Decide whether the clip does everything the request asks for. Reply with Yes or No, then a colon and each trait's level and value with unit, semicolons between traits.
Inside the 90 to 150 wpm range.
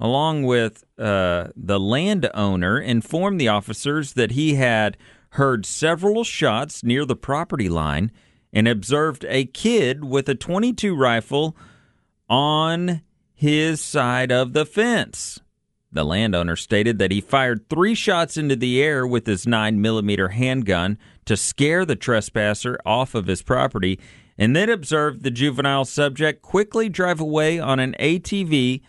Yes: average, 140 wpm